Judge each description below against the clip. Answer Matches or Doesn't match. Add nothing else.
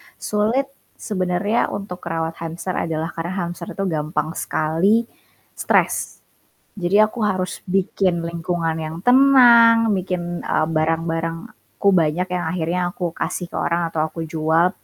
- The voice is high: Doesn't match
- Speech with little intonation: Doesn't match